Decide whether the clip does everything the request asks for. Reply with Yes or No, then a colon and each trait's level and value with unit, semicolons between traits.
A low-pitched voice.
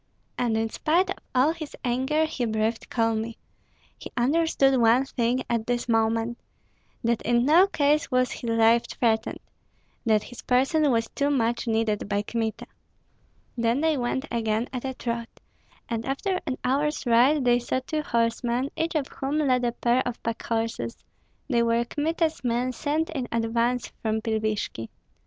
No: high, 240 Hz